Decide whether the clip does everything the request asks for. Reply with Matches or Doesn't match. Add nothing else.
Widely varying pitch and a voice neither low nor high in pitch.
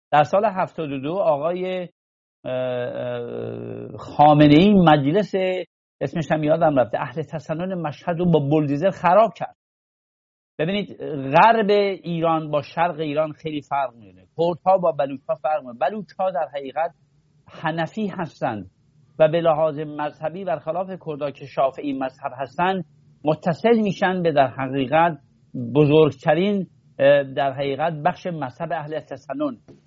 Doesn't match